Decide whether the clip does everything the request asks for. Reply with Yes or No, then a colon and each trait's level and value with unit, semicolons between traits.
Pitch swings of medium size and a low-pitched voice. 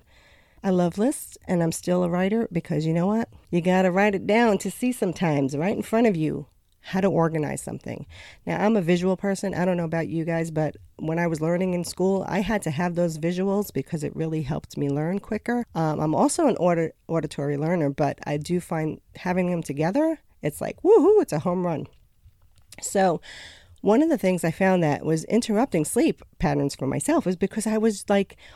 No: average, 4.2 semitones; medium, 175 Hz